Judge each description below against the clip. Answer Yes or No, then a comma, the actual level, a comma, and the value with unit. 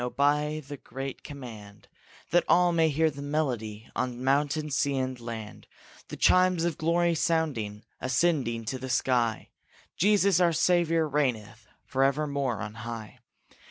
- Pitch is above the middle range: No, medium, 140 Hz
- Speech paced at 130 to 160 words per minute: Yes, average, 140 wpm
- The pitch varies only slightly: No, average, 5.2 semitones